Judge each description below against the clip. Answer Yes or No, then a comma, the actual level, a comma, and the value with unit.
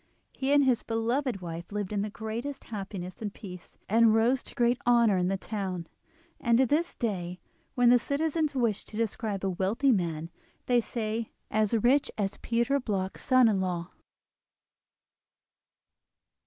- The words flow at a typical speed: Yes, average, 155 wpm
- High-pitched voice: Yes, high, 220 Hz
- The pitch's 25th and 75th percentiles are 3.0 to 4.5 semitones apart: Yes, average, 4.1 semitones